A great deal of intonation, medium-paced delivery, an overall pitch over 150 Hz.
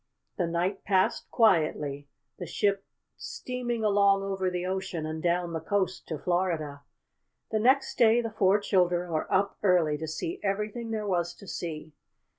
No: average, 3.4 semitones; average, 160 wpm; medium, 185 Hz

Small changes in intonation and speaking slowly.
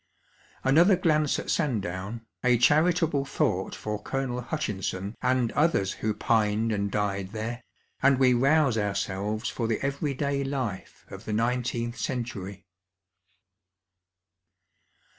No: average, 4.6 semitones; slow, 115 wpm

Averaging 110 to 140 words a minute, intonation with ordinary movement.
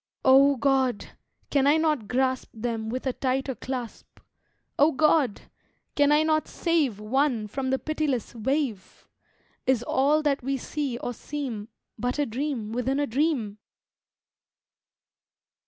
Yes: slow, 135 wpm; average, 3.2 semitones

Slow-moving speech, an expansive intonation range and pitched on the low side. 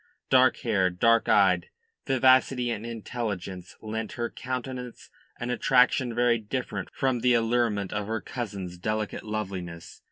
No: slow, 130 wpm; average, 3.2 semitones; low, 115 Hz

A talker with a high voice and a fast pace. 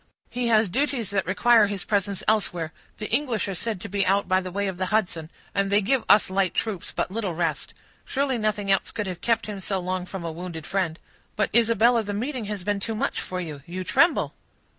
Yes: high, 200 Hz; fast, 225 wpm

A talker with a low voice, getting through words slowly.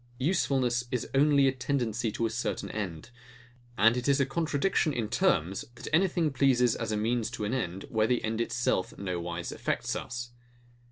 No: low, 120 Hz; average, 175 wpm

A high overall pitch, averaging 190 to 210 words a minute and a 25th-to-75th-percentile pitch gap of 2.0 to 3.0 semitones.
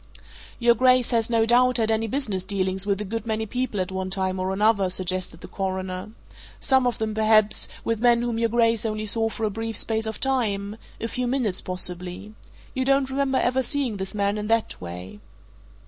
No: high, 220 Hz; average, 195 wpm; average, 3.7 semitones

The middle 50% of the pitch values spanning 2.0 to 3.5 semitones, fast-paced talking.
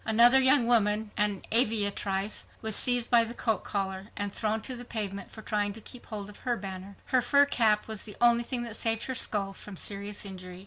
Yes: average, 2.9 semitones; fast, 215 wpm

